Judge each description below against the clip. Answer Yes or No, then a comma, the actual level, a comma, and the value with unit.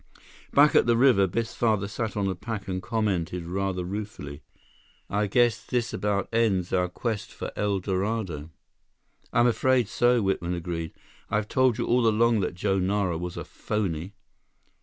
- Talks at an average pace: Yes, average, 160 wpm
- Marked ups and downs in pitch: No, average, 3.9 semitones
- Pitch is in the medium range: No, low, 100 Hz